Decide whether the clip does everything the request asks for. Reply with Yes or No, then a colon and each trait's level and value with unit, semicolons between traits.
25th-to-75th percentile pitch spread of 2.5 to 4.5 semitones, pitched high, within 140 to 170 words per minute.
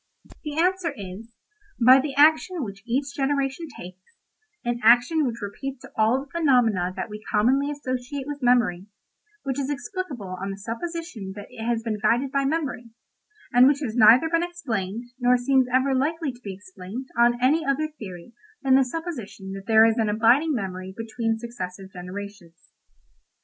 No: average, 5.1 semitones; high, 245 Hz; average, 160 wpm